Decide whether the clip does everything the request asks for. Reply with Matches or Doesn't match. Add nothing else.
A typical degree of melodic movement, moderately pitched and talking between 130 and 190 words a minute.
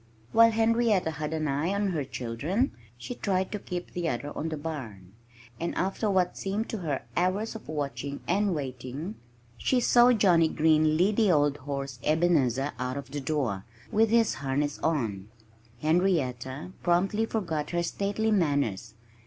Doesn't match